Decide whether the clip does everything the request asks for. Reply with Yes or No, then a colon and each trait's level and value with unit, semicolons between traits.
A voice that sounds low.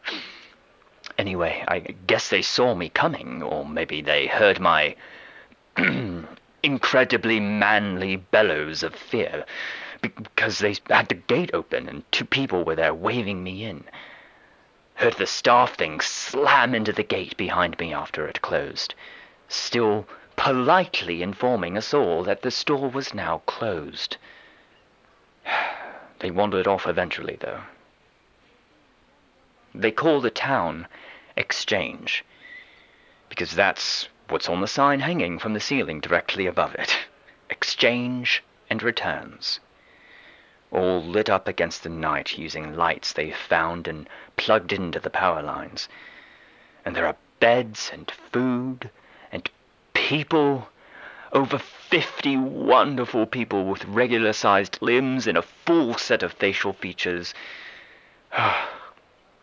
Yes: low, 115 Hz